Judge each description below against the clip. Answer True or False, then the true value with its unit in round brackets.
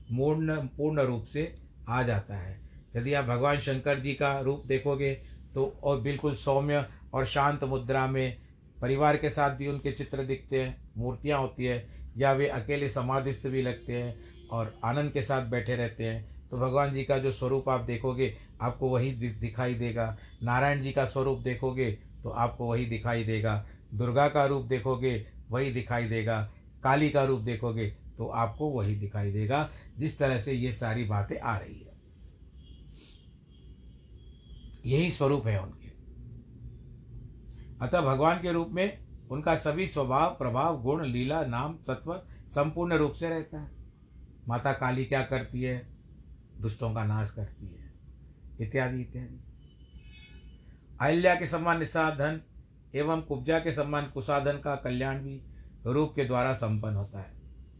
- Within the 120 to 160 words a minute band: True (150 wpm)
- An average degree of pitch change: True (4.0 semitones)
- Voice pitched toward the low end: True (130 Hz)